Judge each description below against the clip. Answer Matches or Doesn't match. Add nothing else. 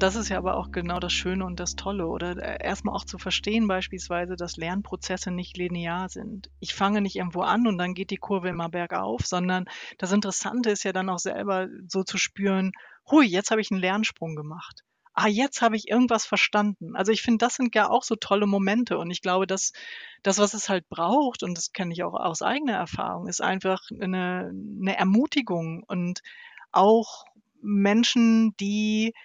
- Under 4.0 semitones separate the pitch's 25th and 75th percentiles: Matches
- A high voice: Matches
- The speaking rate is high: Matches